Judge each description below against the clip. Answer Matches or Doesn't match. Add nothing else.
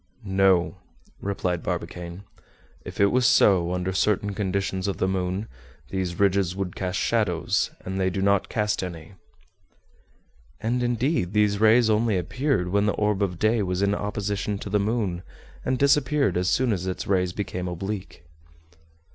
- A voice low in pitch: Matches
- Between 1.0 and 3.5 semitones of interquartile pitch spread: Matches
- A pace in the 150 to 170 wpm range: Matches